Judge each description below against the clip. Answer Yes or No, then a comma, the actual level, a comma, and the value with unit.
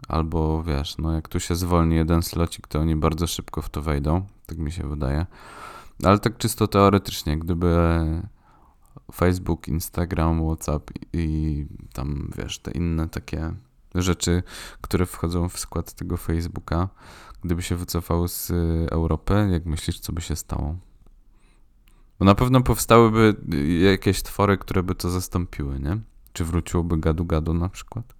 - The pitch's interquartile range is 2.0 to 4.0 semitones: Yes, average, 3.1 semitones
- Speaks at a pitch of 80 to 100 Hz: Yes, very low, 85 Hz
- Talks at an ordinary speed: Yes, average, 150 wpm